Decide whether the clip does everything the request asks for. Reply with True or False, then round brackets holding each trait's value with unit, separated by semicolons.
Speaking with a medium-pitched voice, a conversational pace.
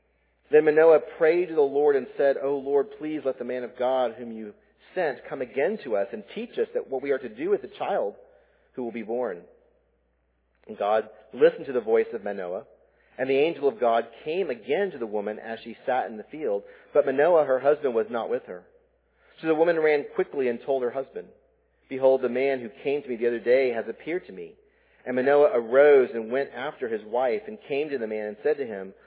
False (155 Hz; 230 wpm)